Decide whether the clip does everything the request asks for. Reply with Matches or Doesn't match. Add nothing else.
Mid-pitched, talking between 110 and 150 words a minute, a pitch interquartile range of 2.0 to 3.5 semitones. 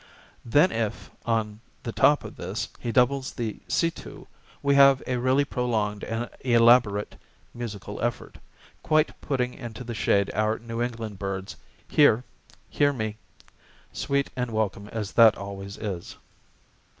Doesn't match